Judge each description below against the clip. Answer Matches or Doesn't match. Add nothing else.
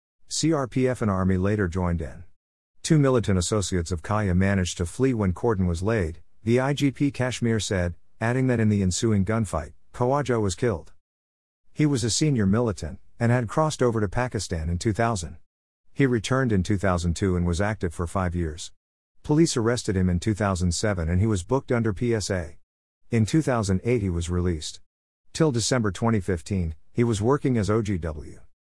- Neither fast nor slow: Matches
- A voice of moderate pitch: Doesn't match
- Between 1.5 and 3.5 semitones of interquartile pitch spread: Doesn't match